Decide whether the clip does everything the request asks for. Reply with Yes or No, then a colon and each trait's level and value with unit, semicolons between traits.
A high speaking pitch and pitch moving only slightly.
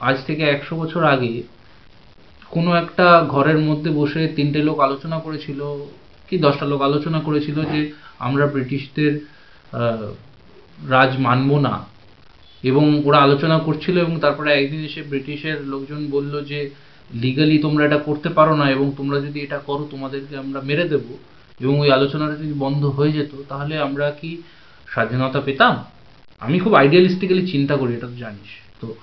No: medium, 145 Hz; narrow, 1.9 semitones